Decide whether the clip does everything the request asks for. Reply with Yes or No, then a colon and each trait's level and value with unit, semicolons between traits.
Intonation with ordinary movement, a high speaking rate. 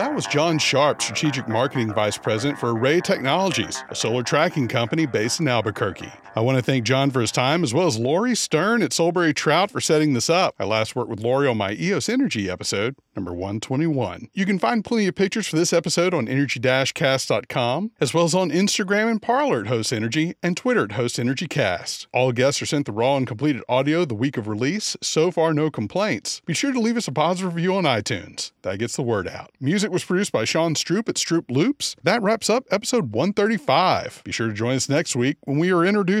No: wide, 6.7 semitones; fast, 220 wpm